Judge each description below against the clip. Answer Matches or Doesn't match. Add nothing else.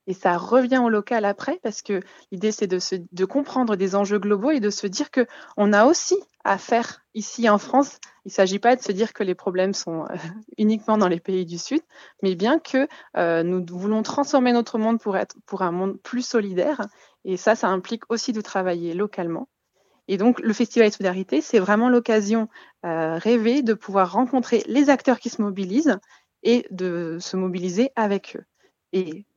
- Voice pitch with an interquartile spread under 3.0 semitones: Doesn't match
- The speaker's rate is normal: Matches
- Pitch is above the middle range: Matches